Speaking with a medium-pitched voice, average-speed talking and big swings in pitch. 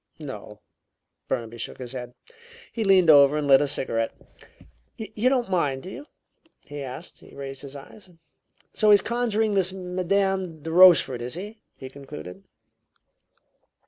Yes: medium, 160 Hz; average, 145 wpm; wide, 6.6 semitones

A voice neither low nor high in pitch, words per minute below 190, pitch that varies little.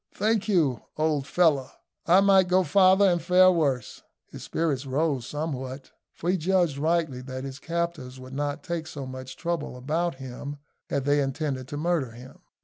No: medium, 150 Hz; average, 170 wpm; average, 4.6 semitones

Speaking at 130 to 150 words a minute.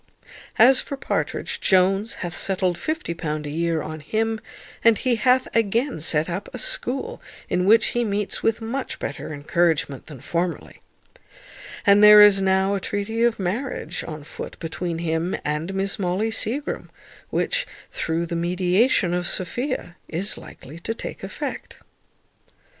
Yes: average, 145 wpm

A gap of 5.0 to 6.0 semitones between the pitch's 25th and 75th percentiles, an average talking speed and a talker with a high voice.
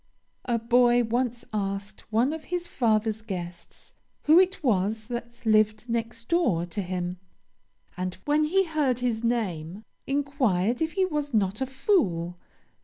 Yes: wide, 5.5 semitones; average, 145 wpm; high, 235 Hz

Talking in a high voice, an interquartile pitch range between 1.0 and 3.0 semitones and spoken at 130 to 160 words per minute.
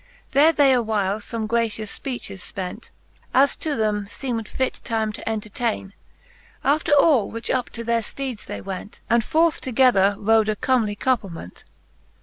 No: high, 225 Hz; average, 3.8 semitones; average, 150 wpm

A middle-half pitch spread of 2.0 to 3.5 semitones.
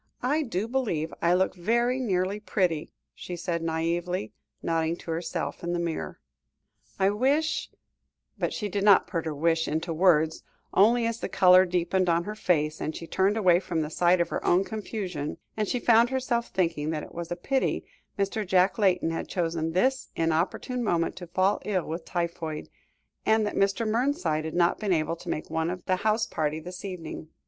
No: average, 4.1 semitones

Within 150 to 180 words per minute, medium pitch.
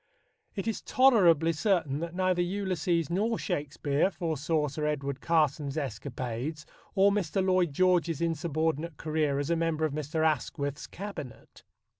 No: slow, 135 wpm; medium, 160 Hz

